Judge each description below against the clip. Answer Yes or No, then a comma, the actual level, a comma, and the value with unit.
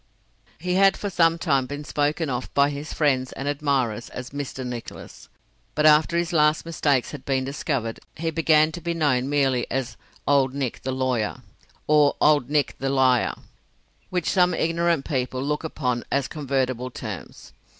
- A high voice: No, medium, 140 Hz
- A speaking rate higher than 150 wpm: Yes, average, 165 wpm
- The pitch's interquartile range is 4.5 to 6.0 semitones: No, average, 3.1 semitones